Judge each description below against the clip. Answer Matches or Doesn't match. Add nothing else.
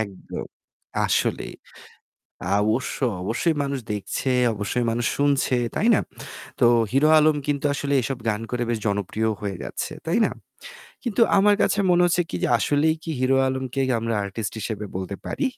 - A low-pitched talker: Matches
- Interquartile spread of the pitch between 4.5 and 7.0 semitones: Matches